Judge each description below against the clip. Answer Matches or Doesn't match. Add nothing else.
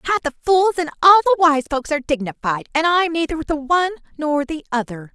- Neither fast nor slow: Doesn't match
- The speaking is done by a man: Doesn't match